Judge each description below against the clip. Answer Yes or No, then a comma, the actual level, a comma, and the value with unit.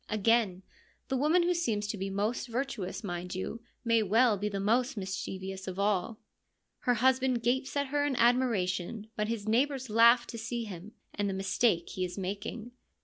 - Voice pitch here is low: No, high, 220 Hz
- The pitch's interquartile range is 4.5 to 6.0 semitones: No, average, 4.1 semitones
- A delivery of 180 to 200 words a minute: Yes, average, 185 wpm